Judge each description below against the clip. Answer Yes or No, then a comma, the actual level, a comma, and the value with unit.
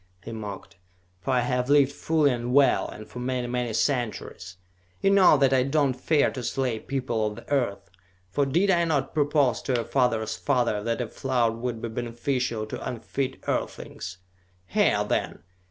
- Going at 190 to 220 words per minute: No, average, 180 wpm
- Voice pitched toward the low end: Yes, low, 125 Hz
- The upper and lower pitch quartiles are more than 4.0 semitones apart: No, average, 3.3 semitones